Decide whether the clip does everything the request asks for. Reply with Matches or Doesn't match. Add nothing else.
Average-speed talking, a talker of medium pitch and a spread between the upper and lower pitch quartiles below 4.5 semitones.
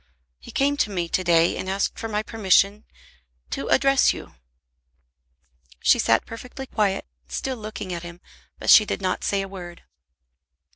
Doesn't match